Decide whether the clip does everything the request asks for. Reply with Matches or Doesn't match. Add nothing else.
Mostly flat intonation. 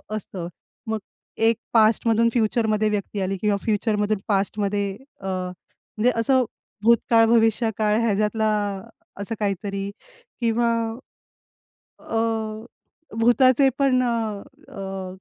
Matches